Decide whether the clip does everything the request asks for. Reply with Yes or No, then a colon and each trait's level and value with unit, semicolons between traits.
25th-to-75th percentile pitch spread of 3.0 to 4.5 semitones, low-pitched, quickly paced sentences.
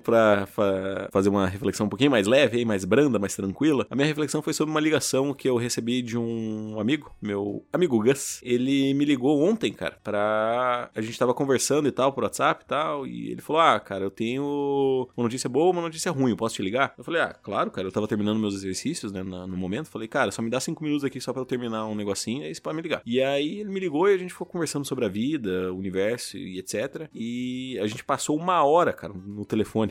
No: average, 5.2 semitones; low, 120 Hz; fast, 235 wpm